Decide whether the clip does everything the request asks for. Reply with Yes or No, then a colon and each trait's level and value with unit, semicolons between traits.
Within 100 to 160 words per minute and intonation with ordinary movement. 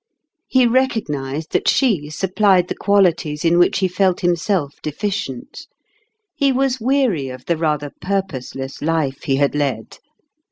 No: average, 145 wpm; wide, 5.8 semitones